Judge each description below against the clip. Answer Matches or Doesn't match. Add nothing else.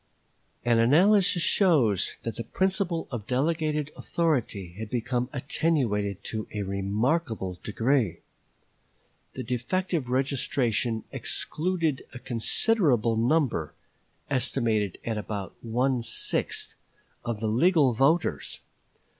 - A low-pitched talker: Matches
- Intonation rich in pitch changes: Matches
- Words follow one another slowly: Matches